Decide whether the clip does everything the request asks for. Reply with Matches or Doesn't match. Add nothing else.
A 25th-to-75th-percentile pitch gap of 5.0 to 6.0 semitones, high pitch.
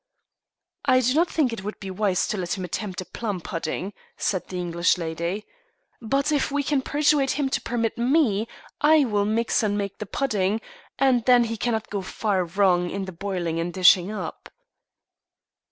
Matches